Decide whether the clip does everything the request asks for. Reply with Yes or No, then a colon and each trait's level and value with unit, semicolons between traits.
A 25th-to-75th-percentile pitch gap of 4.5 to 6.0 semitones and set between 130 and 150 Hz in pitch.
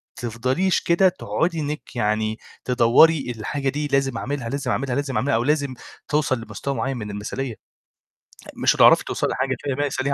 No: average, 3.4 semitones; low, 135 Hz